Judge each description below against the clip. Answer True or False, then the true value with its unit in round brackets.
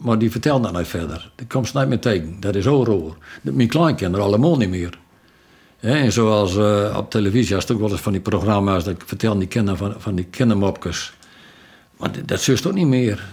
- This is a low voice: True (105 Hz)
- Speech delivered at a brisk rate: True (225 wpm)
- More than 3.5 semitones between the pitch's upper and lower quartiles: True (4.3 semitones)